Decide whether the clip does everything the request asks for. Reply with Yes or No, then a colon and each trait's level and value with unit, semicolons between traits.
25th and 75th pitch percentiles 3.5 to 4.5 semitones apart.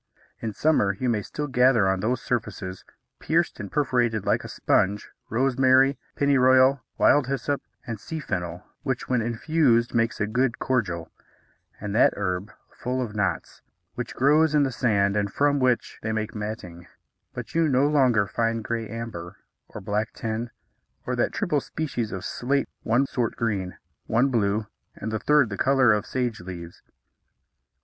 Yes: average, 4.0 semitones